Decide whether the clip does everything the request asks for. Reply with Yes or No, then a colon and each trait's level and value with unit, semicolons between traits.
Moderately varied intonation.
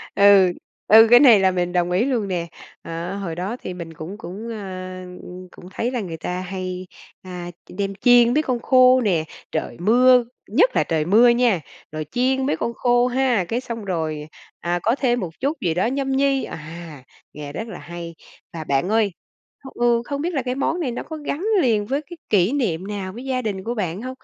No: wide, 5.8 semitones